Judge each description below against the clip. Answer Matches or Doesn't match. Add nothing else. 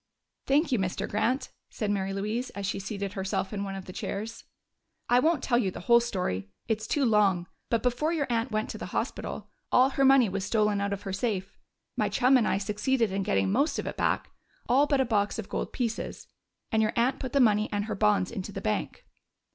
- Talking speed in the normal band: Doesn't match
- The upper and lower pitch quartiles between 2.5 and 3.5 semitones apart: Doesn't match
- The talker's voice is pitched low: Doesn't match